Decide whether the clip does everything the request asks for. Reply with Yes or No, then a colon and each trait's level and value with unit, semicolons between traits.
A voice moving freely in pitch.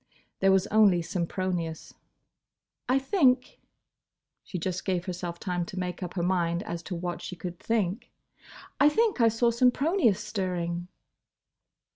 No: average, 4.6 semitones